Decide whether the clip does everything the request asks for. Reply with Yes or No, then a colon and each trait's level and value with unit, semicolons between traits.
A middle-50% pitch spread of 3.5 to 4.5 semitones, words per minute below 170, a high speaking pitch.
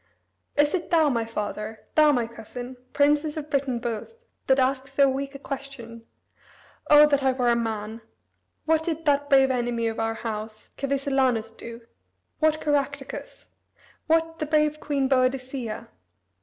Yes: average, 3.9 semitones; average, 150 wpm; very high, 270 Hz